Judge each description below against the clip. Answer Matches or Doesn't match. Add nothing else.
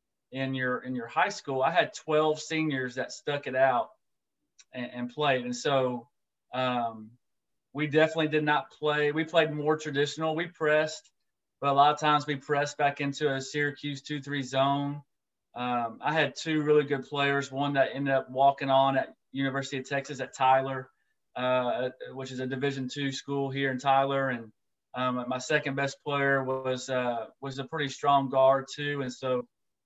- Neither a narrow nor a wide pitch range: Doesn't match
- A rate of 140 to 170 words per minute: Doesn't match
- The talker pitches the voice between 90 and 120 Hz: Doesn't match